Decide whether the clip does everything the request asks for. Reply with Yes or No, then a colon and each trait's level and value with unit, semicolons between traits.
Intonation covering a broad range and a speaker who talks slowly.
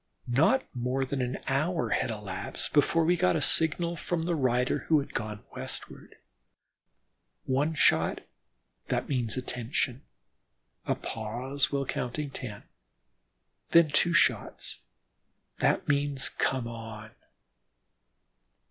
No: average, 4.2 semitones; slow, 110 wpm